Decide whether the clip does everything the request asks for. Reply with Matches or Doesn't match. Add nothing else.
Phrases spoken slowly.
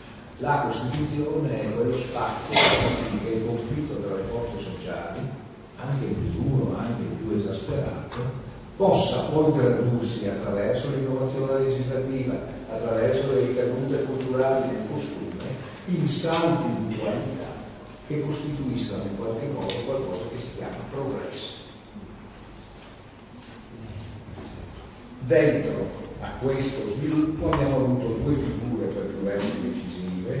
Matches